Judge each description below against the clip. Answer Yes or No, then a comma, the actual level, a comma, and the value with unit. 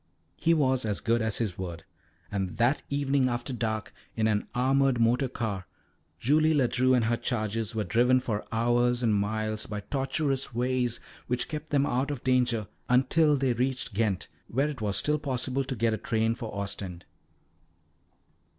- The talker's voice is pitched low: Yes, low, 120 Hz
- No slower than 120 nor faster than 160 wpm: No, average, 170 wpm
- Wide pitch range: No, average, 3.4 semitones